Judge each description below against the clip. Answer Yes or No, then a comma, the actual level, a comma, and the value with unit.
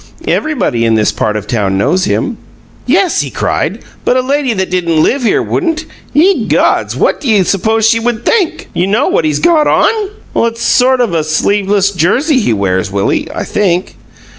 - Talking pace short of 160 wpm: No, average, 190 wpm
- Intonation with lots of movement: Yes, wide, 8.8 semitones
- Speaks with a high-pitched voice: Yes, high, 210 Hz